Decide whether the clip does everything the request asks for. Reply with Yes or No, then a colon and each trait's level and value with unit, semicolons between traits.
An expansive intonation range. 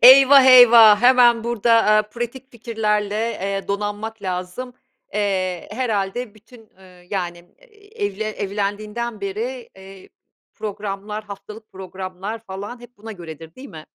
No: average, 3.4 semitones